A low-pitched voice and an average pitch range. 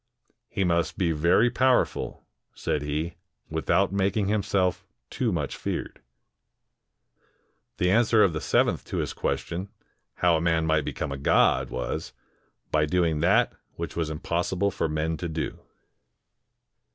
Yes: very low, 85 Hz; average, 3.8 semitones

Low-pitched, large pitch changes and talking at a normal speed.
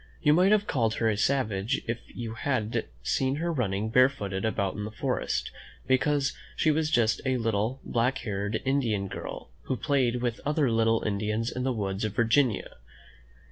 No: low, 115 Hz; average, 4.0 semitones; average, 180 wpm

